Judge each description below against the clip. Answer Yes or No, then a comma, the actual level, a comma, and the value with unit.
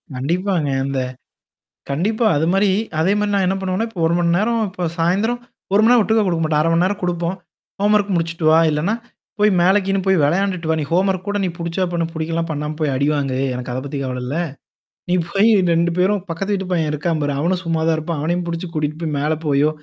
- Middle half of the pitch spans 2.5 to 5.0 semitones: Yes, average, 3.9 semitones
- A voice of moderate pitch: Yes, medium, 170 Hz